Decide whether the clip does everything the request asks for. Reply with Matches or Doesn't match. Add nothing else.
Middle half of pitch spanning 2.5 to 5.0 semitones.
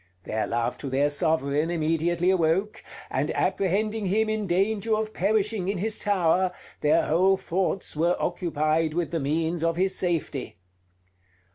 Matches